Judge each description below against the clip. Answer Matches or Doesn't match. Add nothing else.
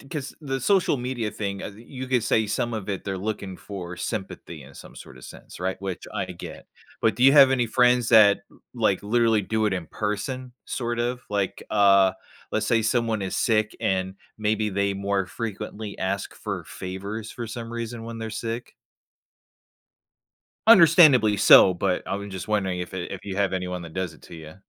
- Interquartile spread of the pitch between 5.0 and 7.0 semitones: Doesn't match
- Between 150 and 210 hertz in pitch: Doesn't match